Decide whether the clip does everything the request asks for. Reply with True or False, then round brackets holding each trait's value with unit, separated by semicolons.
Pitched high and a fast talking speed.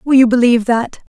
True (240 Hz; 210 wpm)